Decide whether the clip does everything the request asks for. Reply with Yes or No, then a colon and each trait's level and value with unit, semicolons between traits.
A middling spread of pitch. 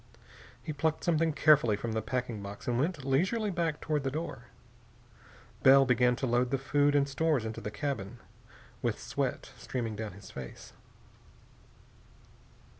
Yes: average, 4.5 semitones